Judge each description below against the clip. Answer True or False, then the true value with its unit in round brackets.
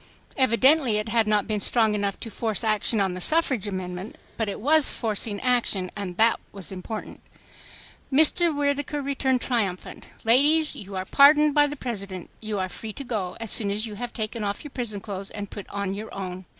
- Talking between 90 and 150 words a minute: False (195 wpm)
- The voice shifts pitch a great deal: False (4.6 semitones)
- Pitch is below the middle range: False (220 Hz)